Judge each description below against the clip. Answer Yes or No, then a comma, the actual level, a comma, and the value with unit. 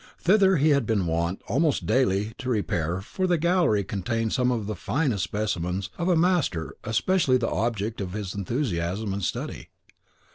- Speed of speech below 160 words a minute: No, average, 170 wpm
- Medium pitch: No, low, 110 Hz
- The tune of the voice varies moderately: No, wide, 6.5 semitones